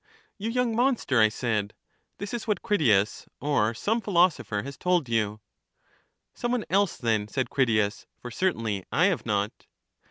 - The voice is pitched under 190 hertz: Yes, low, 135 Hz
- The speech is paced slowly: No, average, 155 wpm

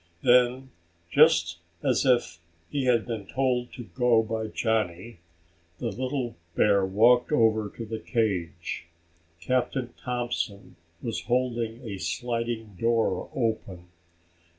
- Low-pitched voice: Yes, low, 115 Hz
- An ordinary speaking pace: No, slow, 115 wpm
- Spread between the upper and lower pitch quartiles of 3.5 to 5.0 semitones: No, average, 2.7 semitones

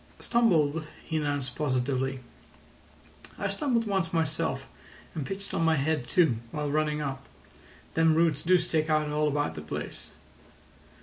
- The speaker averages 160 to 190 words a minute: No, average, 140 wpm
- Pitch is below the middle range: No, medium, 155 Hz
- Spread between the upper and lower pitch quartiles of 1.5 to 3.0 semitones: Yes, narrow, 2.6 semitones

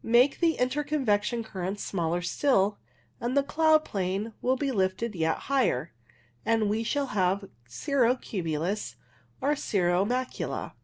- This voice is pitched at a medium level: No, high, 220 Hz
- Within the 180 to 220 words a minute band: No, slow, 135 wpm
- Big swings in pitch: Yes, wide, 5.9 semitones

